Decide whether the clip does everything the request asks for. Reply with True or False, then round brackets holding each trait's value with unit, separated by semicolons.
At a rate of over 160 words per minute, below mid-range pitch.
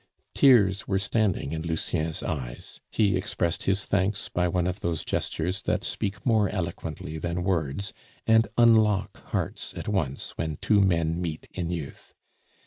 False (150 wpm; 90 Hz)